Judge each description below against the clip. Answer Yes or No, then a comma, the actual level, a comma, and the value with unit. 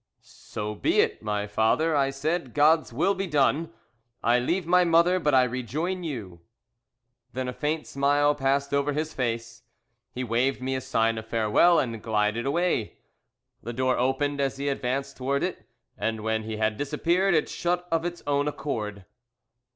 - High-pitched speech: No, low, 135 Hz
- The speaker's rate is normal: Yes, average, 170 wpm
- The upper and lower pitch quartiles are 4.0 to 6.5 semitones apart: Yes, average, 5.3 semitones